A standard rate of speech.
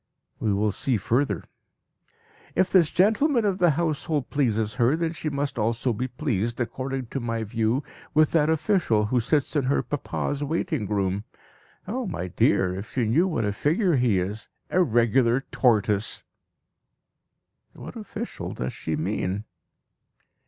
Yes: average, 150 wpm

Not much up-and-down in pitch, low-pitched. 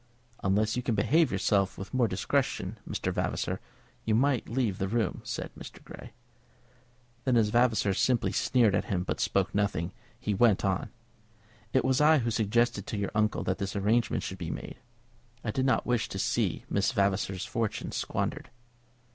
No: average, 3.6 semitones; low, 110 Hz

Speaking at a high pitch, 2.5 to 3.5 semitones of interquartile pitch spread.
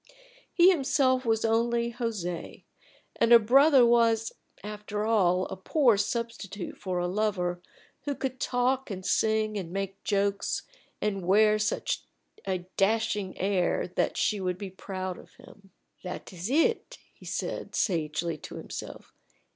No: high, 210 Hz; average, 3.9 semitones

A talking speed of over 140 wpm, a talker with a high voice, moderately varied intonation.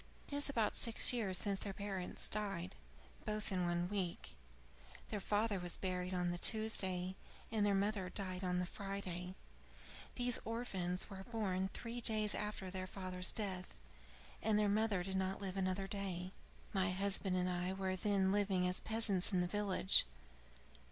No: average, 165 wpm; high, 195 Hz; narrow, 2.3 semitones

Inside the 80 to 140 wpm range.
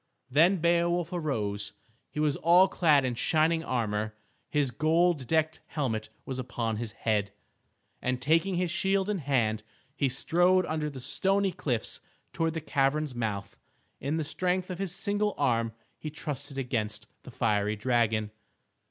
No: average, 150 wpm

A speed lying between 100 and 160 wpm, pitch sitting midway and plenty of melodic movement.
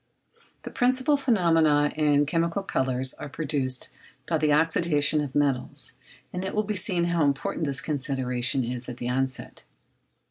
No: average, 150 wpm; medium, 150 Hz; average, 4.3 semitones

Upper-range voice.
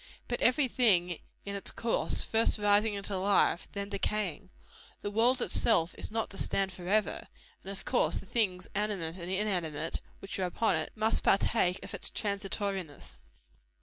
Yes: high, 200 Hz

